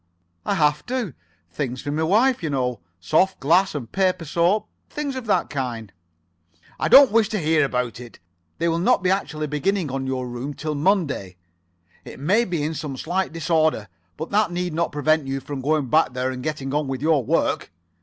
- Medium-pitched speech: Yes, medium, 155 Hz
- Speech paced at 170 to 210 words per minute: Yes, average, 195 wpm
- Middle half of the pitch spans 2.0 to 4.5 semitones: No, wide, 5.4 semitones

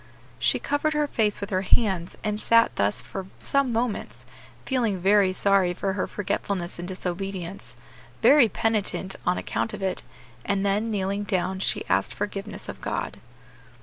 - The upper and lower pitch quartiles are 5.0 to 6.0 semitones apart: No, narrow, 2.6 semitones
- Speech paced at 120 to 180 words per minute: Yes, average, 155 wpm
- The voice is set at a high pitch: Yes, high, 200 Hz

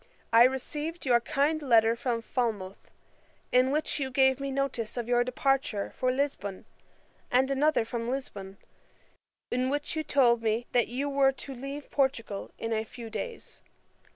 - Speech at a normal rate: Yes, average, 155 wpm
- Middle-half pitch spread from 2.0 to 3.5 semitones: Yes, average, 3.1 semitones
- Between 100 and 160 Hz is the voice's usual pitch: No, very high, 255 Hz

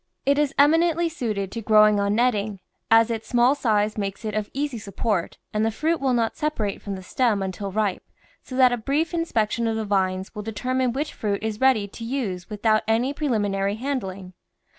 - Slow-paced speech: No, average, 195 wpm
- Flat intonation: No, average, 4.1 semitones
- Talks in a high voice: Yes, high, 220 Hz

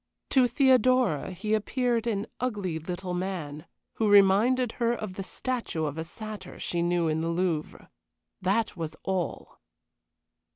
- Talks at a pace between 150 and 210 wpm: No, average, 140 wpm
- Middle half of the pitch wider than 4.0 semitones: Yes, average, 5.1 semitones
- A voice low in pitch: No, high, 195 Hz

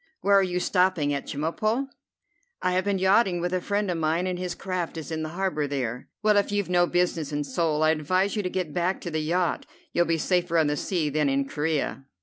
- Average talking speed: No, fast, 235 wpm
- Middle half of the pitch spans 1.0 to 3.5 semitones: Yes, average, 3.2 semitones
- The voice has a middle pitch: Yes, medium, 175 Hz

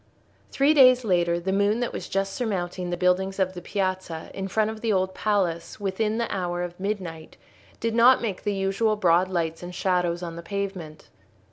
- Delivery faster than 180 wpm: Yes, average, 195 wpm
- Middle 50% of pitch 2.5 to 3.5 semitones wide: Yes, average, 3.2 semitones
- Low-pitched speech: No, high, 190 Hz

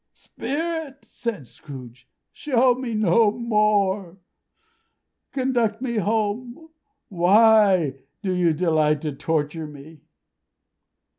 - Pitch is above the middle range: Yes, high, 205 Hz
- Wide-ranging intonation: Yes, wide, 6.7 semitones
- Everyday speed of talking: No, slow, 90 wpm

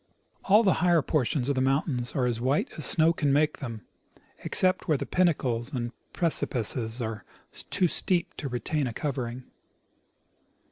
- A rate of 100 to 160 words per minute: Yes, average, 150 wpm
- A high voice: No, low, 135 Hz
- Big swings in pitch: No, average, 5.0 semitones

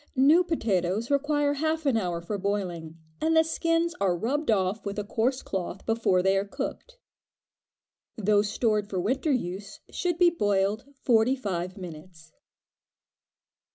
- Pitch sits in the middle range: No, high, 210 Hz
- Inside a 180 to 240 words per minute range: No, average, 145 wpm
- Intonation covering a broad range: Yes, wide, 6.9 semitones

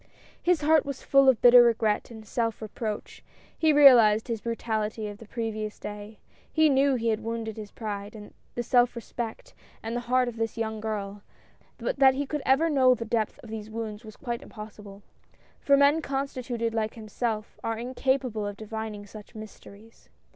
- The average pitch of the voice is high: Yes, high, 225 Hz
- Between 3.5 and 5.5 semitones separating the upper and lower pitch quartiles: No, average, 2.9 semitones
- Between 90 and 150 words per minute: No, average, 185 wpm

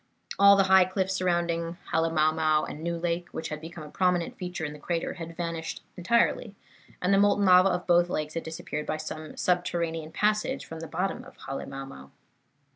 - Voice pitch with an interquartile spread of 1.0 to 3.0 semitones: Yes, narrow, 2.6 semitones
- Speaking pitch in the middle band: Yes, medium, 170 Hz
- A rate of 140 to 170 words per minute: No, average, 185 wpm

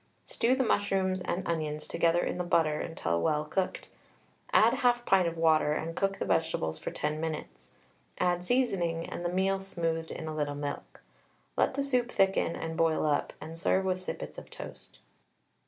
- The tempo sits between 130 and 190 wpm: Yes, average, 180 wpm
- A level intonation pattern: No, average, 3.6 semitones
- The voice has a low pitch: No, medium, 165 Hz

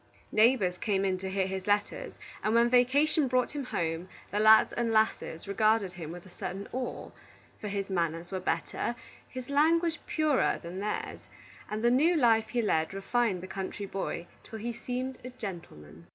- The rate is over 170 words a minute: Yes, average, 180 wpm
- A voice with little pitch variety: No, average, 4.8 semitones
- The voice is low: No, high, 215 Hz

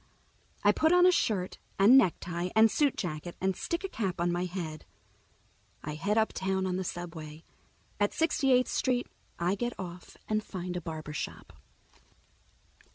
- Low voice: No, medium, 185 Hz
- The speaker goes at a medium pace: Yes, average, 160 wpm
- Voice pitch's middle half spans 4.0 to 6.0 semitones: Yes, average, 4.5 semitones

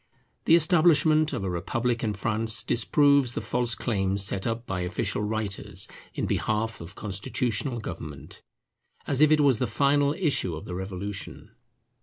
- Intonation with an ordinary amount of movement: No, wide, 6.2 semitones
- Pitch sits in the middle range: No, low, 115 Hz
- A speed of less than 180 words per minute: Yes, average, 155 wpm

